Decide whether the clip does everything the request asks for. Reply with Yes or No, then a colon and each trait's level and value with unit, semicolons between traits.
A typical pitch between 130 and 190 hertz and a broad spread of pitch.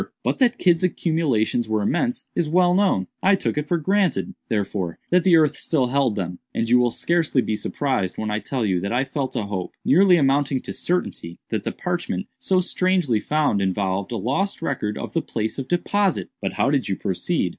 Yes: medium, 140 Hz; wide, 8.7 semitones